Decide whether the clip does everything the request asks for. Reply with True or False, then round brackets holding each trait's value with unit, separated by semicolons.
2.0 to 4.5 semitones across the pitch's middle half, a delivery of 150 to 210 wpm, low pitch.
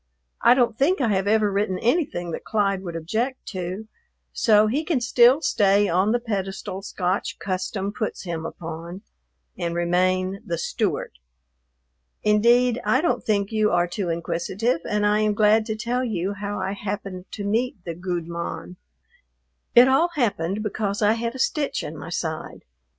False (3.9 semitones; 165 wpm; 205 Hz)